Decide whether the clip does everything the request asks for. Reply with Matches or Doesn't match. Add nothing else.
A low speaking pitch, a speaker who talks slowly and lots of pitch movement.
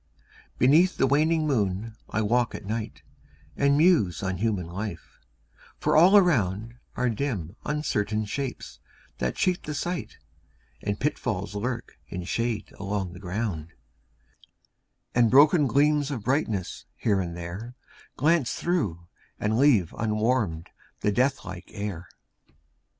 Matches